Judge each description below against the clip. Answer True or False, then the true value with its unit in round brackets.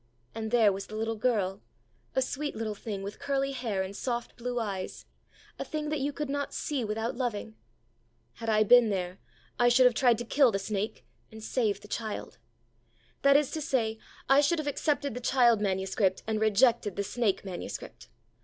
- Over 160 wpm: True (190 wpm)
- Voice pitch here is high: True (225 Hz)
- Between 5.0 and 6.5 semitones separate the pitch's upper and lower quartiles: False (4.0 semitones)